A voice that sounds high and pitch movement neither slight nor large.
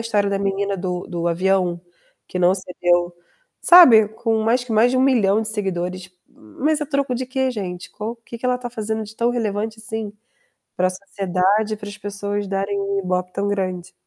Yes: high, 205 Hz; average, 3.5 semitones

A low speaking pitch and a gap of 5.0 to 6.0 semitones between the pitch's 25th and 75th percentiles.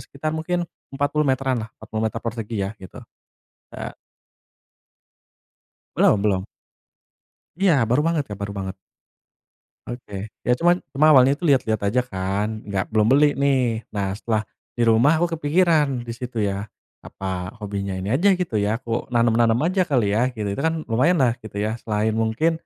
Yes: low, 115 Hz; wide, 5.5 semitones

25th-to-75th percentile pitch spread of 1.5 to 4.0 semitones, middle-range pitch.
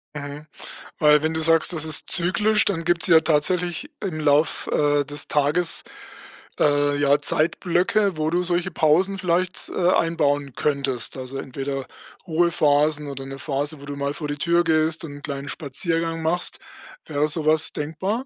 Yes: average, 2.9 semitones; medium, 155 Hz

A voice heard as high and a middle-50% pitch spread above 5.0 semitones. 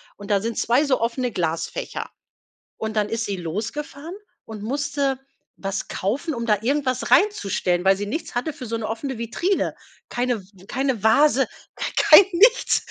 Yes: high, 235 Hz; wide, 5.4 semitones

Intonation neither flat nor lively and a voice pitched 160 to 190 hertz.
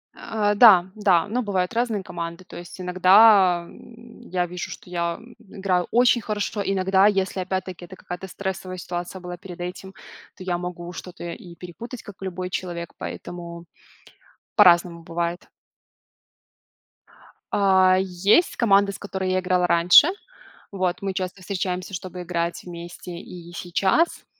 No: narrow, 1.9 semitones; medium, 185 Hz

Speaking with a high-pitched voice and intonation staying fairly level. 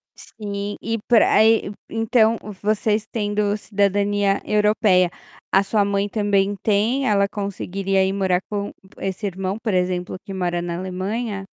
Yes: high, 200 Hz; narrow, 1.6 semitones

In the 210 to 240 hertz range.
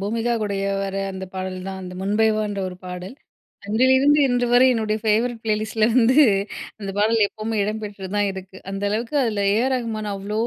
Yes: high, 215 Hz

